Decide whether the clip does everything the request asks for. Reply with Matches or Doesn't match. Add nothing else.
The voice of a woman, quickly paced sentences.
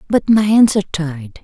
Matches